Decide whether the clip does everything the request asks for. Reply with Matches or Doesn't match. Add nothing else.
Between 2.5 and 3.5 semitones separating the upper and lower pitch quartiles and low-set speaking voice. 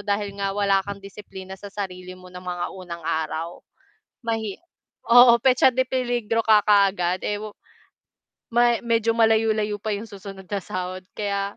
Doesn't match